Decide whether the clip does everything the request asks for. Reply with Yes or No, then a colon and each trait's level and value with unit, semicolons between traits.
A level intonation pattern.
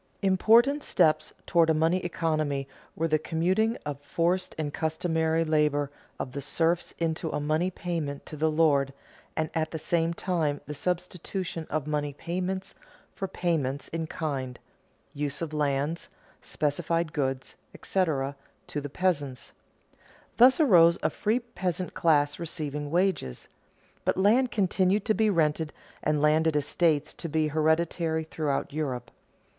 No: average, 3.1 semitones